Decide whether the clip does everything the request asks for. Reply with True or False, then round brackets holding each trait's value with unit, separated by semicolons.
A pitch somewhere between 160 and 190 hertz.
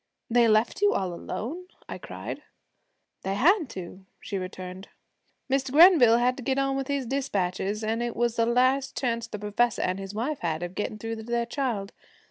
False (235 Hz)